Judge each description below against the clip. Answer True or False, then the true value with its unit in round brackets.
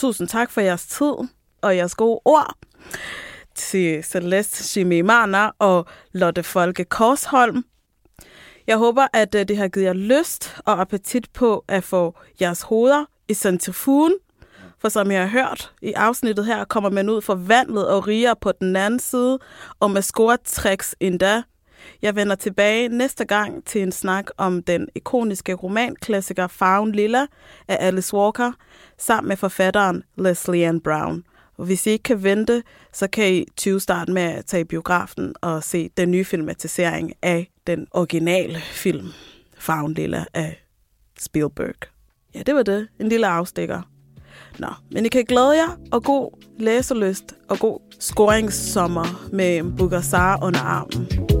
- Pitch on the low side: False (200 Hz)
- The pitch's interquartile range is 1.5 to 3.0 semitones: False (4.0 semitones)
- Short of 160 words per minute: True (150 wpm)